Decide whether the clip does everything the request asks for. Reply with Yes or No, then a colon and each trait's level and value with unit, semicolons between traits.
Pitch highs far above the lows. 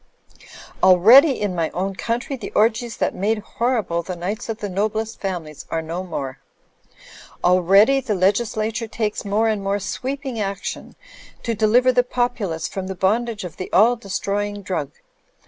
No: average, 3.8 semitones